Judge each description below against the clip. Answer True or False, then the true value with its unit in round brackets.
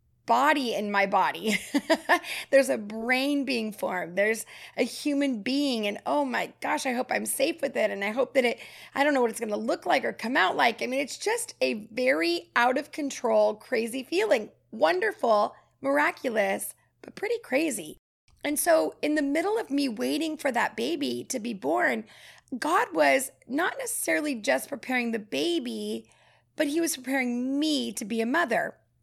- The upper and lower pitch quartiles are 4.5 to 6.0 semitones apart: True (4.9 semitones)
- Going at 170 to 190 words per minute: True (180 wpm)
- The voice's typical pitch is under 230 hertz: False (270 Hz)